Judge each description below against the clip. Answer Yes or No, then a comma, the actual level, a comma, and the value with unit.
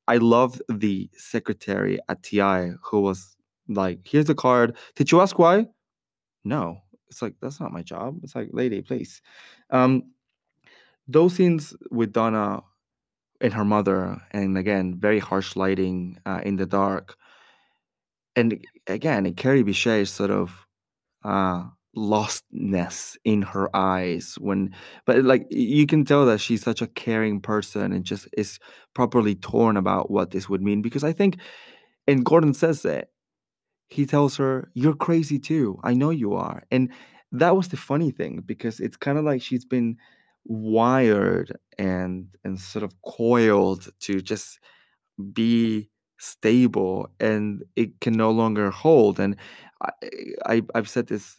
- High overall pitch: No, low, 110 Hz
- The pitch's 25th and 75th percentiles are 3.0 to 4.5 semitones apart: No, average, 5.0 semitones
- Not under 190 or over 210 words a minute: No, average, 150 wpm